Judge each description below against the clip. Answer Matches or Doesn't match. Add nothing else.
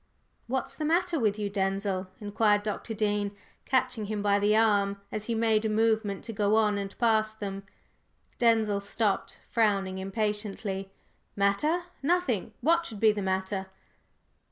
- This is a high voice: Matches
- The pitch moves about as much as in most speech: Doesn't match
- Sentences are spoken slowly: Doesn't match